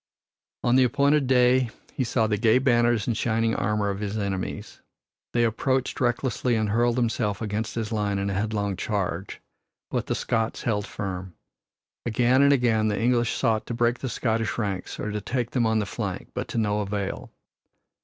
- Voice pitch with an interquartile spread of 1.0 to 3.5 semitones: Yes, average, 2.7 semitones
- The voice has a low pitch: Yes, low, 115 Hz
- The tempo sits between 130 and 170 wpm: No, average, 185 wpm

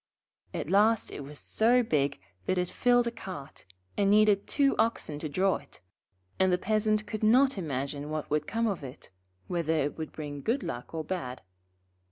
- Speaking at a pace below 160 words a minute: No, average, 185 wpm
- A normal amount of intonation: No, wide, 6.6 semitones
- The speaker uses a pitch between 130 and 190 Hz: Yes, medium, 185 Hz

